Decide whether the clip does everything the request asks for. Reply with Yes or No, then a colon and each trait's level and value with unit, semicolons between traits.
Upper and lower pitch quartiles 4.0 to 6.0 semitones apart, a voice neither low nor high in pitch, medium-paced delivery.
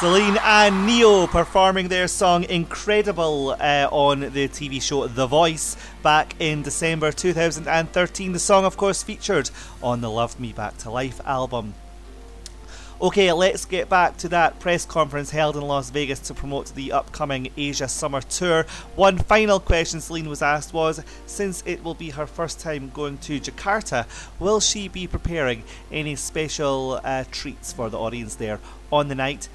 Yes: average, 5.0 semitones; medium, 150 Hz; average, 165 wpm